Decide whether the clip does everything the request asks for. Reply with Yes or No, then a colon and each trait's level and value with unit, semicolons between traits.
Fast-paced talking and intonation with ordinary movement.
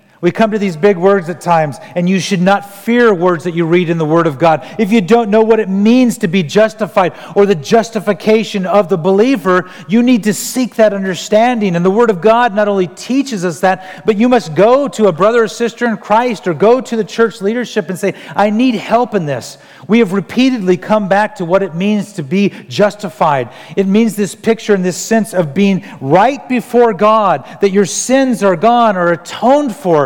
Yes: fast, 220 wpm; average, 3.5 semitones